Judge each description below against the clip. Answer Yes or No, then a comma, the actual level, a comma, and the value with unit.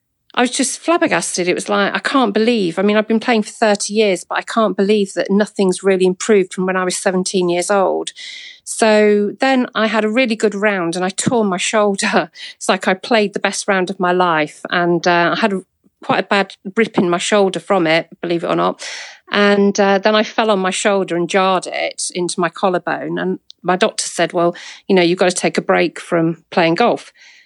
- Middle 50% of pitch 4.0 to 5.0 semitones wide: No, average, 3.2 semitones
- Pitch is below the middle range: No, high, 200 Hz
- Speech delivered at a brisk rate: Yes, fast, 225 wpm